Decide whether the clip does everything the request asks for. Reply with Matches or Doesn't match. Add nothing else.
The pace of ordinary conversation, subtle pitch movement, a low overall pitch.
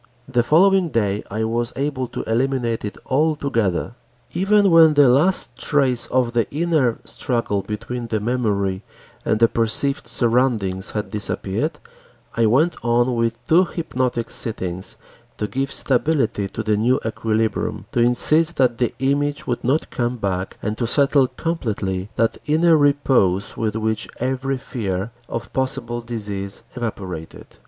Doesn't match